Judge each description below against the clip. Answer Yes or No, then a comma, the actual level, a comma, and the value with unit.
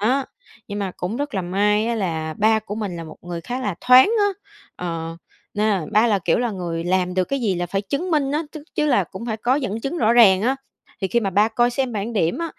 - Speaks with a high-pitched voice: Yes, high, 210 Hz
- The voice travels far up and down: No, average, 5.0 semitones